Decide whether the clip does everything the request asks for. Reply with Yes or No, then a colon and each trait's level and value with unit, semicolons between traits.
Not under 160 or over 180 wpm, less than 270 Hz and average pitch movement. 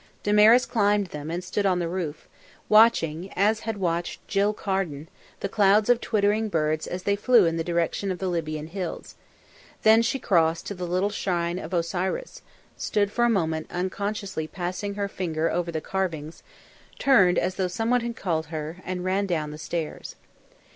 Yes: average, 175 wpm; medium, 185 Hz; average, 3.6 semitones